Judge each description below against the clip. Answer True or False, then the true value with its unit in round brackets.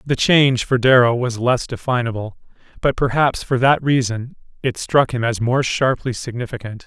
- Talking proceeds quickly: False (165 wpm)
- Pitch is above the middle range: False (125 Hz)